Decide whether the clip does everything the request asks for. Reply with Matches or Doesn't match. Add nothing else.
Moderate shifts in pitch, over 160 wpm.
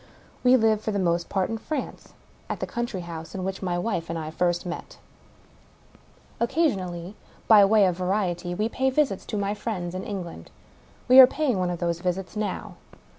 Matches